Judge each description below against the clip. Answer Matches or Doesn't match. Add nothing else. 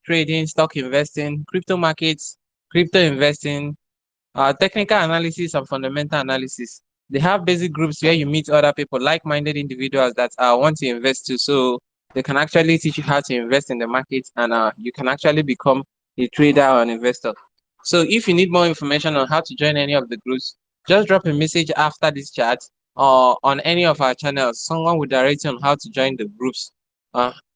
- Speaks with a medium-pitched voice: Matches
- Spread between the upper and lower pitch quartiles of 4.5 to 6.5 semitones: Doesn't match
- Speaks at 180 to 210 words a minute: Matches